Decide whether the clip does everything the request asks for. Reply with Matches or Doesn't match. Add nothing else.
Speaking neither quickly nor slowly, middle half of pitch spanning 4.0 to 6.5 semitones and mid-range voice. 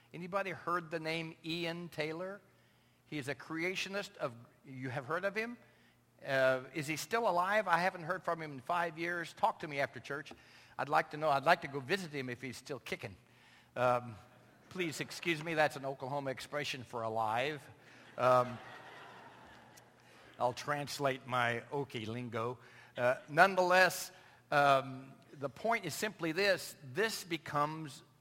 Matches